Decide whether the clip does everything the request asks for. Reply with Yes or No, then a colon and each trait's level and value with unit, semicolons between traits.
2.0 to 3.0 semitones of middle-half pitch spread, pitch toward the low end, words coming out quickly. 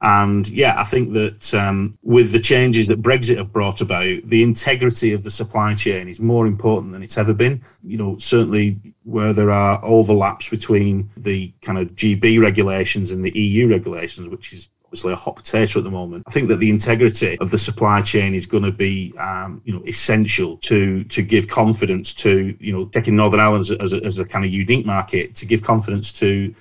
Yes: narrow, 2.4 semitones; low, 105 Hz; fast, 210 wpm